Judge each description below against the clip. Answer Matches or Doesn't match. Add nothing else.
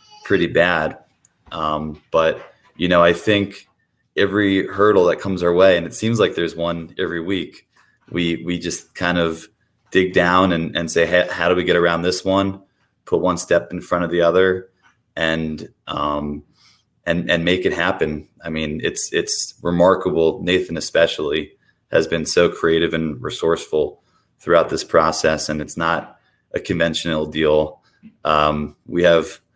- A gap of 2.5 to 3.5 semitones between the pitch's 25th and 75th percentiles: Matches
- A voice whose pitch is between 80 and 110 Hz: Matches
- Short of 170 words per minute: Matches